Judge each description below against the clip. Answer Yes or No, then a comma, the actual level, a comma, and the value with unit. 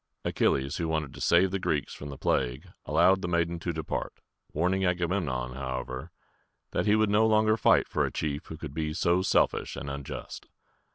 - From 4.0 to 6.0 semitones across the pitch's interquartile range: Yes, average, 4.9 semitones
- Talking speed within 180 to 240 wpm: Yes, average, 185 wpm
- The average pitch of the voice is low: Yes, very low, 80 Hz